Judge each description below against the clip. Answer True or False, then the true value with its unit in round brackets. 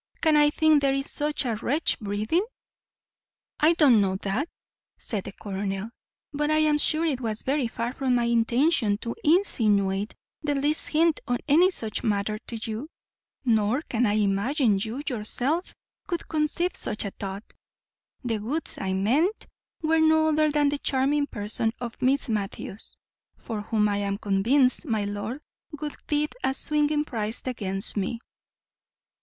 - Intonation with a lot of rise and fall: True (6.1 semitones)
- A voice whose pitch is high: True (245 Hz)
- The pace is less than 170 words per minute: True (160 wpm)